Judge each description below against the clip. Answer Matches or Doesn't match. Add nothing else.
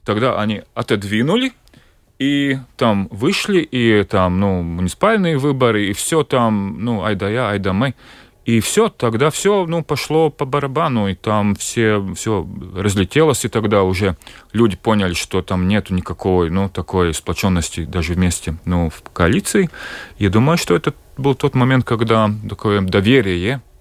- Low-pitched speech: Matches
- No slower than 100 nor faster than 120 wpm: Doesn't match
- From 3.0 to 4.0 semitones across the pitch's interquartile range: Doesn't match